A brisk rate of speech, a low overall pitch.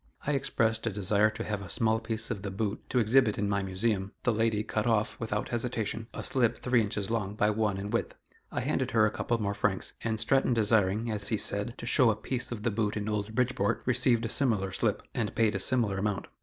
Yes: fast, 235 wpm; low, 110 Hz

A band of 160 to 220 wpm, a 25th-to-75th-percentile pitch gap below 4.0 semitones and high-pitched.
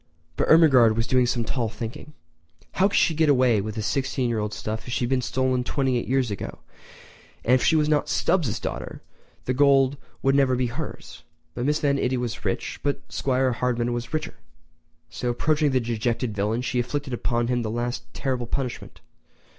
No: average, 195 wpm; narrow, 2.6 semitones; low, 125 Hz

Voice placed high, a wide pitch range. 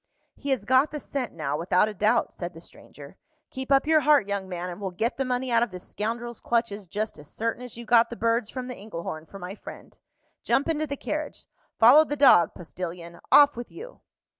Yes: high, 230 Hz; wide, 6.3 semitones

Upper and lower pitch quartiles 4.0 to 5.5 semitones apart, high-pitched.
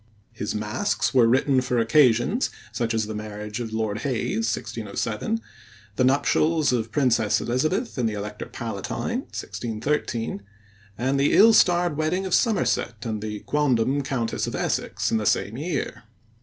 No: average, 4.7 semitones; low, 120 Hz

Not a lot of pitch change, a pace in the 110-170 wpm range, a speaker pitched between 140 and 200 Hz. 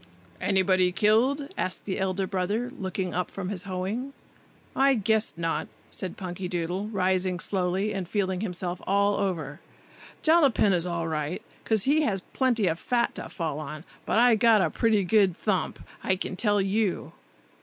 No: average, 3.2 semitones; average, 155 wpm; high, 190 Hz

